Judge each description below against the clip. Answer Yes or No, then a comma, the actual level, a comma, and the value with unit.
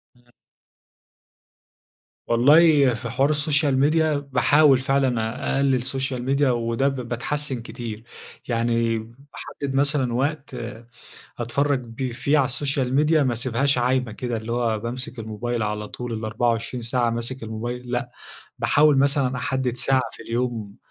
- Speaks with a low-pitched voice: Yes, low, 125 Hz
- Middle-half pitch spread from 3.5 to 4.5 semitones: No, average, 2.9 semitones